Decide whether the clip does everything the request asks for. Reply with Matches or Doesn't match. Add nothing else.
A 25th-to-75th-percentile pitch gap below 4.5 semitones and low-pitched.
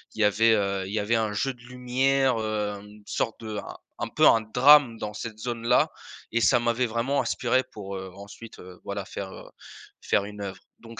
Matches